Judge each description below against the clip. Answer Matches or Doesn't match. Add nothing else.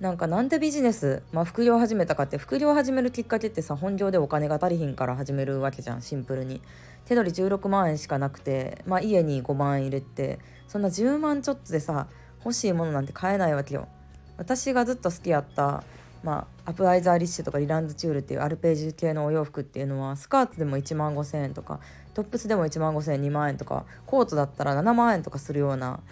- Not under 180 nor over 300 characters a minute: Doesn't match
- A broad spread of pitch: Matches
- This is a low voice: Doesn't match